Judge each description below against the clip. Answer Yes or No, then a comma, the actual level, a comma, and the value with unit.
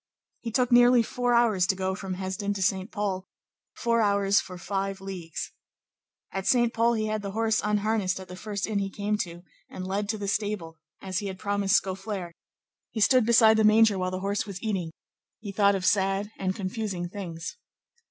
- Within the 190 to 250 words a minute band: Yes, average, 195 wpm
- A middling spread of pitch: No, narrow, 2.3 semitones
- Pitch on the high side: Yes, high, 200 Hz